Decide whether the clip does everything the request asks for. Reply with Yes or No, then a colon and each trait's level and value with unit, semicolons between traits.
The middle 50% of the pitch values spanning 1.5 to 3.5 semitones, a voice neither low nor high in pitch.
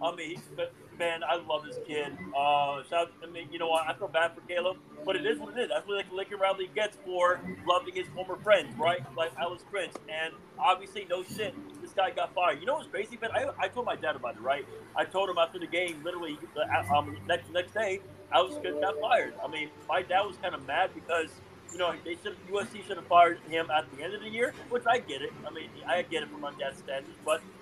Yes: average, 2.8 semitones; medium, 180 Hz